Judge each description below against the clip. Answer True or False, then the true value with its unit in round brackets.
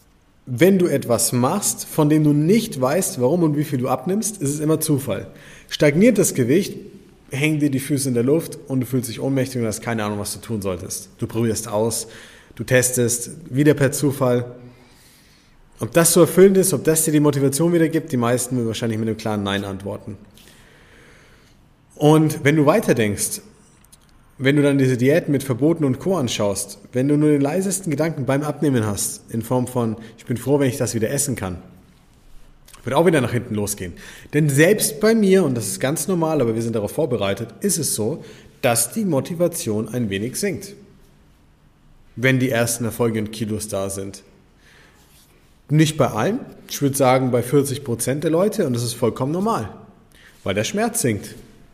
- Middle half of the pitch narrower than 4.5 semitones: False (5.2 semitones)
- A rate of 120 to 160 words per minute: False (190 wpm)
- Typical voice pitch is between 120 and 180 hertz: True (130 Hz)